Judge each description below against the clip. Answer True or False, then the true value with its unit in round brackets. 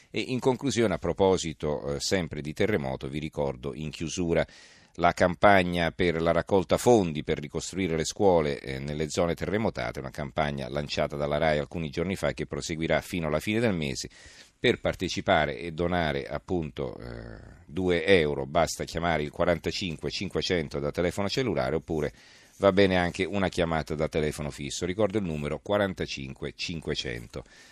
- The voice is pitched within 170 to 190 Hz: False (80 Hz)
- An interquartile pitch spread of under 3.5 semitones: False (3.8 semitones)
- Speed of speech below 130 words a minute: False (155 wpm)